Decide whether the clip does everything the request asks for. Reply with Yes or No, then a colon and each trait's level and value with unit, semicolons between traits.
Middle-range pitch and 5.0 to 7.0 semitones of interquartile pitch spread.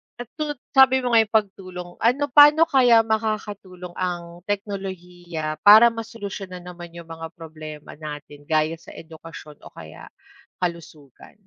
Yes: medium, 180 Hz; wide, 5.4 semitones